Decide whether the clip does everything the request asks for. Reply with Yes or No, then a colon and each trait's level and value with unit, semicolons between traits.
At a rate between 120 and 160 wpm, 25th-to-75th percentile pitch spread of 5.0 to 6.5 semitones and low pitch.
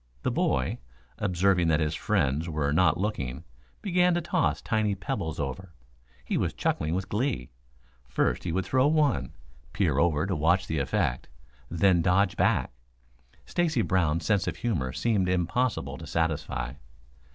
Yes: average, 150 wpm; average, 5.3 semitones; very low, 90 Hz